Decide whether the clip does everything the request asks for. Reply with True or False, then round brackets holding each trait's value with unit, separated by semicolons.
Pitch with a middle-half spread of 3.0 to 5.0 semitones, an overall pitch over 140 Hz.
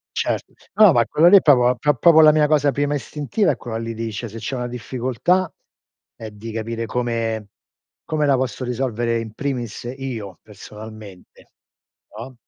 False (4.1 semitones; 120 Hz)